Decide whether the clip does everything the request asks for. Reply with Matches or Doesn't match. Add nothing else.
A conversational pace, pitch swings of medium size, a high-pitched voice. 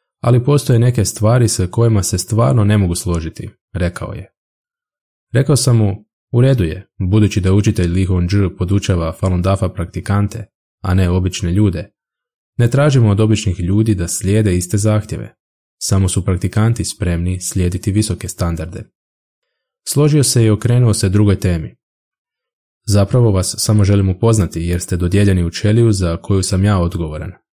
Doesn't match